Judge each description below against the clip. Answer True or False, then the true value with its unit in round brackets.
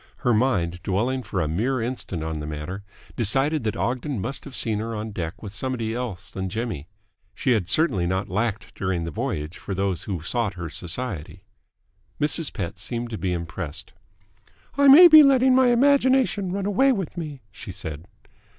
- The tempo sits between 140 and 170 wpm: False (180 wpm)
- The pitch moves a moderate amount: False (7.8 semitones)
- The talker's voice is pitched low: True (110 Hz)